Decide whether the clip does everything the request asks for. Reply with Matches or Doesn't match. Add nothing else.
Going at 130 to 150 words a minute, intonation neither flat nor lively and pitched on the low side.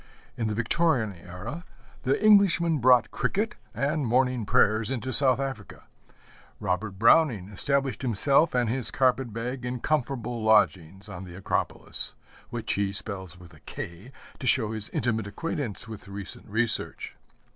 Matches